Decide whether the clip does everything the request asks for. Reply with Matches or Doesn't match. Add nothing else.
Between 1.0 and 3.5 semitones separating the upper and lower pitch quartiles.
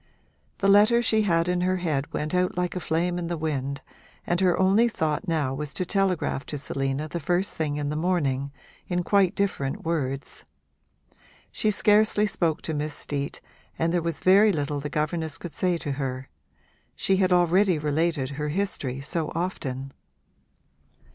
Doesn't match